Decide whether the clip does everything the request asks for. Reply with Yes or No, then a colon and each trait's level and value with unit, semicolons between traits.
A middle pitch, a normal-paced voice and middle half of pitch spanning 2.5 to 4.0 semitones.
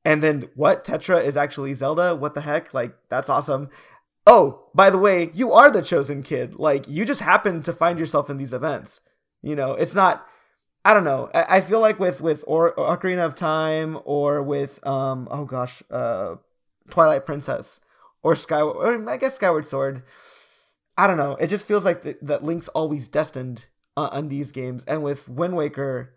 Yes: medium, 155 Hz; average, 185 wpm; average, 3.5 semitones